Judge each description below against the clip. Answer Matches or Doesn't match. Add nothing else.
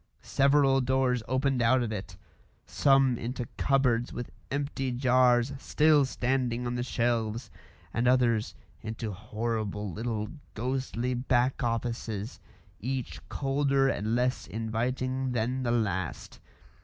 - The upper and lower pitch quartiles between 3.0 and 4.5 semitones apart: Doesn't match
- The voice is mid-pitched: Doesn't match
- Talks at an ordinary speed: Doesn't match